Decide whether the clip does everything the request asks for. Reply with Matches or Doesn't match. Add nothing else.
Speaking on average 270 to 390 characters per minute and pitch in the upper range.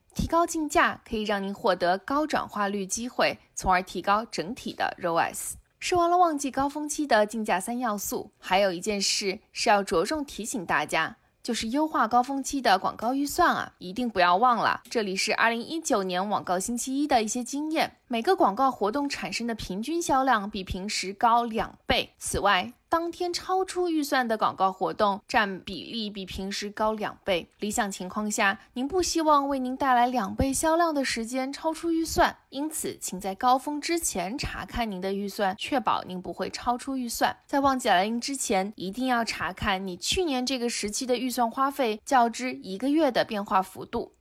Matches